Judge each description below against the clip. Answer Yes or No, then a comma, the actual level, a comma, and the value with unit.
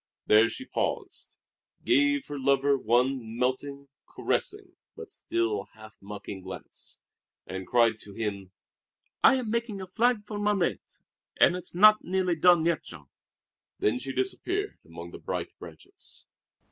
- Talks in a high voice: No, medium, 140 Hz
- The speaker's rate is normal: Yes, average, 145 wpm